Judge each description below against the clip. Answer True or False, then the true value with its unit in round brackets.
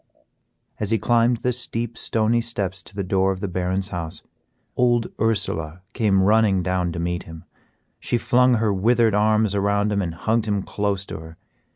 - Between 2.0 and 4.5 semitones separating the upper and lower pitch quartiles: True (3.4 semitones)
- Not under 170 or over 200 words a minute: True (180 wpm)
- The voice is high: False (100 Hz)